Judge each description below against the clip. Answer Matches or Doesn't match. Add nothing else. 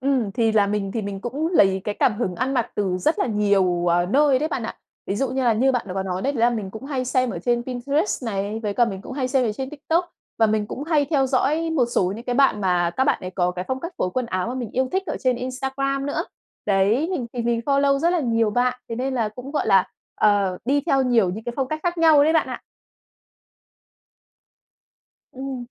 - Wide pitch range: Doesn't match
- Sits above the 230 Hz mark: Matches